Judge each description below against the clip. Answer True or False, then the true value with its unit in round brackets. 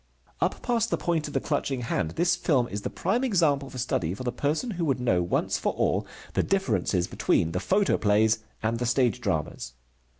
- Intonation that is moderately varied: False (8.5 semitones)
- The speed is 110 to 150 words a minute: False (200 wpm)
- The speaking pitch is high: False (130 Hz)